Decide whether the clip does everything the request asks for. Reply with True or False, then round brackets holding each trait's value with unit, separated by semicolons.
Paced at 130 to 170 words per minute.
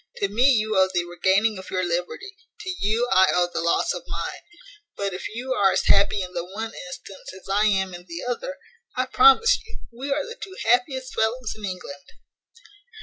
False (200 wpm)